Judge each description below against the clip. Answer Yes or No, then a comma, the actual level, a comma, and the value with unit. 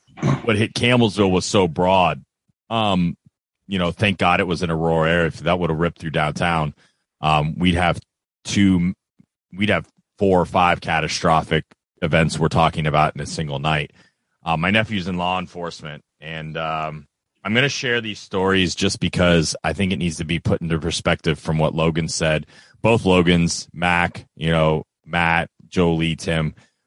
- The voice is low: Yes, very low, 85 Hz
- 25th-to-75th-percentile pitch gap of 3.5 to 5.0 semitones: No, average, 2.8 semitones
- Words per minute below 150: No, average, 175 wpm